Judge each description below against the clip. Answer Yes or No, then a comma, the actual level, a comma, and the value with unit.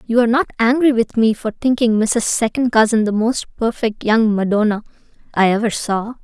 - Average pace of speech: Yes, average, 185 wpm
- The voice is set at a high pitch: Yes, high, 225 Hz